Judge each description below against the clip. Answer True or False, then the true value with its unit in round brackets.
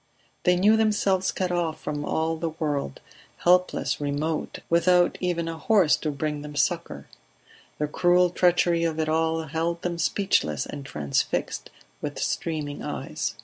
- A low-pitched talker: False (165 Hz)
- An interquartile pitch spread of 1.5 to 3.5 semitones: True (2.9 semitones)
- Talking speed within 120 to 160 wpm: True (145 wpm)